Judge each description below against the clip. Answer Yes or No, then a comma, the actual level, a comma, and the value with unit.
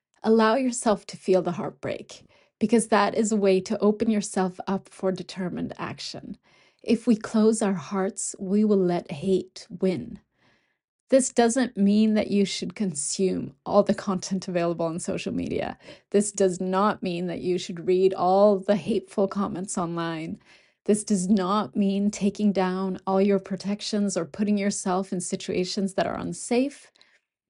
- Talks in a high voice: Yes, high, 195 Hz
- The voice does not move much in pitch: Yes, narrow, 2.0 semitones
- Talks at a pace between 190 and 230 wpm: No, average, 155 wpm